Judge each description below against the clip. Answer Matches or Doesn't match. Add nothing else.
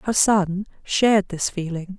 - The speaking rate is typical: Matches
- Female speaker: Matches